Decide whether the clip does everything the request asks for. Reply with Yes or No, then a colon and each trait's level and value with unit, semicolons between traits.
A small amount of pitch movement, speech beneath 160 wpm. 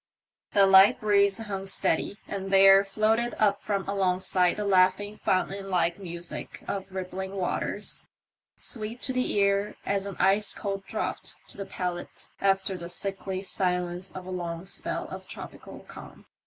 Yes: narrow, 1.4 semitones; average, 150 wpm